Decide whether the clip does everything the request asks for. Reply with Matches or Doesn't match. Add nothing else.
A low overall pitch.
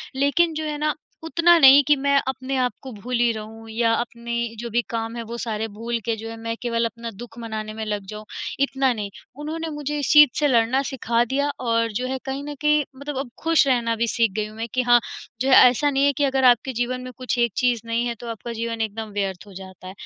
Doesn't match